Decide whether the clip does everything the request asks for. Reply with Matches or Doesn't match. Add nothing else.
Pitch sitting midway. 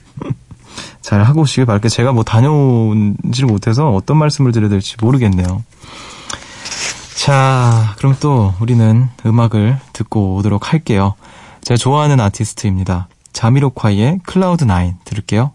Doesn't match